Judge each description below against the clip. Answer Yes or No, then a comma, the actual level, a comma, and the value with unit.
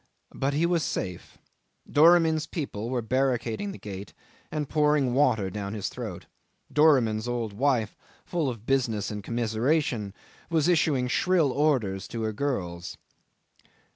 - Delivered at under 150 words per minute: Yes, slow, 135 wpm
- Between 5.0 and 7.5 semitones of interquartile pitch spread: Yes, wide, 5.6 semitones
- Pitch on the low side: Yes, low, 125 Hz